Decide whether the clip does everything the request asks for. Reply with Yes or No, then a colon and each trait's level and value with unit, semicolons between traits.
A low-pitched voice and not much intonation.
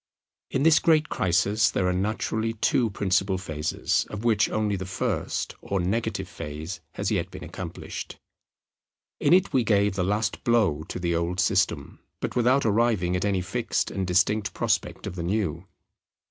No: low, 100 Hz; average, 3.7 semitones